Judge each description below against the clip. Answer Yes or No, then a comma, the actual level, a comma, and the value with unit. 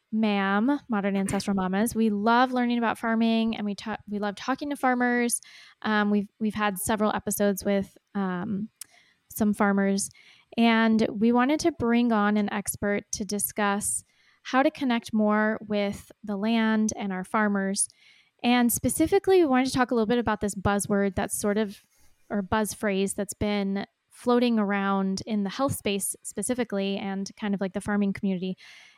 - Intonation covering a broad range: No, narrow, 2.6 semitones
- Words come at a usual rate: Yes, average, 170 wpm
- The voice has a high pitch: Yes, high, 210 Hz